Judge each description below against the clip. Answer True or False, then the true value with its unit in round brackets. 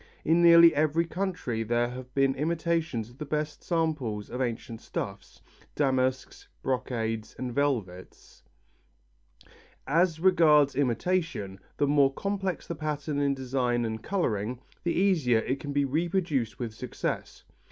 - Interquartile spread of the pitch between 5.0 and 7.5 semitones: True (5.3 semitones)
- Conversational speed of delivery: False (130 wpm)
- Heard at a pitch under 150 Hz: True (140 Hz)